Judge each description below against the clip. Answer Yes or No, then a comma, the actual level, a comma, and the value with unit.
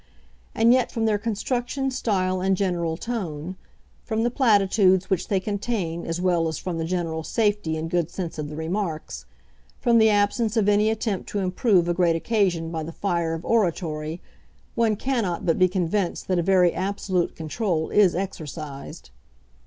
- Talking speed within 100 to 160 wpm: No, average, 170 wpm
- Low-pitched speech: No, medium, 185 Hz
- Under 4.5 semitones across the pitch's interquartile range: Yes, average, 4.1 semitones